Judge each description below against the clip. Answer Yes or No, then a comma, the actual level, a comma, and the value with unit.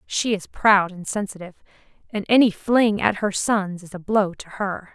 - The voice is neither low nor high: No, high, 200 Hz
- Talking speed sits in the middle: Yes, average, 195 wpm